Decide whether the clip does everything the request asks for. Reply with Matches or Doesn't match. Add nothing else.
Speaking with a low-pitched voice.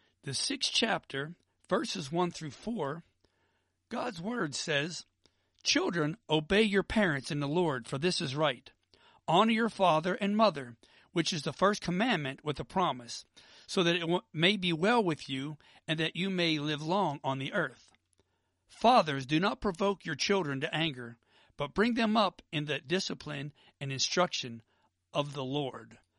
Doesn't match